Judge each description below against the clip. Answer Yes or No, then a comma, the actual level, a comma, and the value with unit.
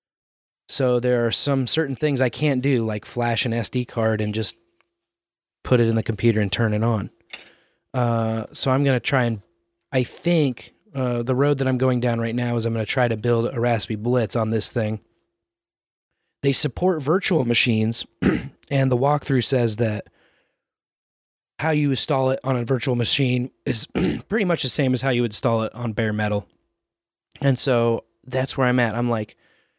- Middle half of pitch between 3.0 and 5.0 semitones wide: No, narrow, 2.6 semitones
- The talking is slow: No, average, 190 wpm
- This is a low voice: Yes, low, 120 Hz